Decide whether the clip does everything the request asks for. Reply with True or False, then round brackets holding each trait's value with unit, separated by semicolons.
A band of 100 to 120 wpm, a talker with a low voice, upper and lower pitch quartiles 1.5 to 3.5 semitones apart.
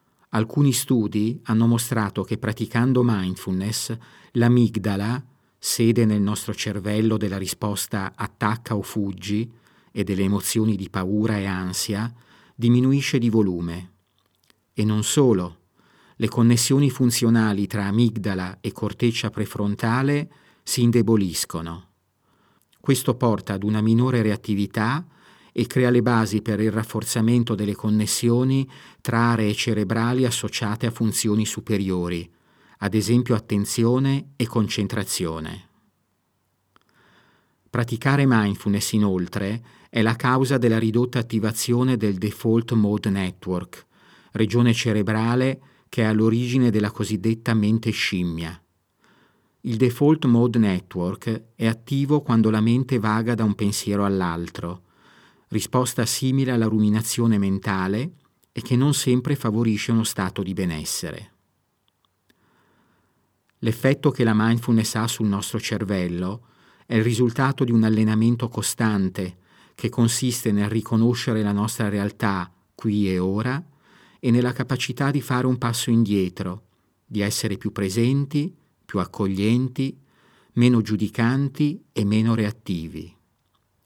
True (115 wpm; 110 Hz; 2.9 semitones)